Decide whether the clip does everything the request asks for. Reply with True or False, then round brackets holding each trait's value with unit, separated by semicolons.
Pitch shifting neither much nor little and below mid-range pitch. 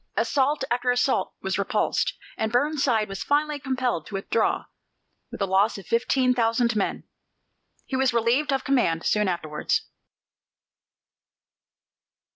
False (4.1 semitones; 240 Hz)